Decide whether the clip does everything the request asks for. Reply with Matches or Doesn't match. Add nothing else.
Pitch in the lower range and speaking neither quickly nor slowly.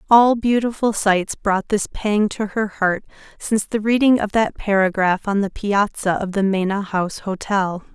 Doesn't match